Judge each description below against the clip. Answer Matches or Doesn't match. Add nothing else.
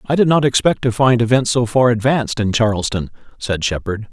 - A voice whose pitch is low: Matches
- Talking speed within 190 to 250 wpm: Matches